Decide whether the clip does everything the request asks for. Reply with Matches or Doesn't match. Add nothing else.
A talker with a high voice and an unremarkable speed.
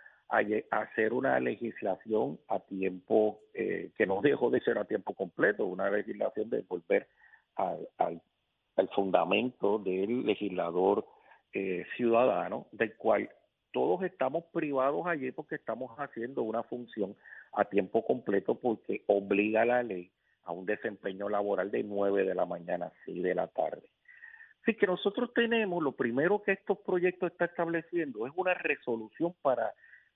Doesn't match